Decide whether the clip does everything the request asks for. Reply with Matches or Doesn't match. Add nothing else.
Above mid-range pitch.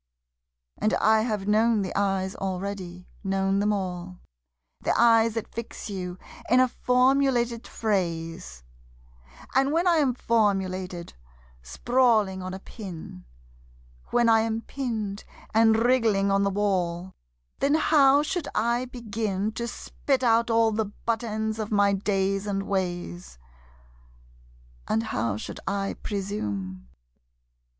Matches